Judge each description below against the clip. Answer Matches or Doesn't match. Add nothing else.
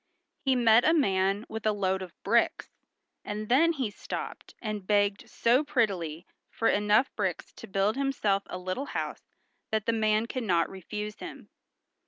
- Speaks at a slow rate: Doesn't match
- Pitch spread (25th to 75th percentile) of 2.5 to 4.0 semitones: Matches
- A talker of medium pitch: Doesn't match